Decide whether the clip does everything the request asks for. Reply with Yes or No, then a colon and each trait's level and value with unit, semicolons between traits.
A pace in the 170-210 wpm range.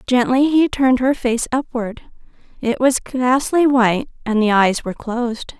No: average, 160 wpm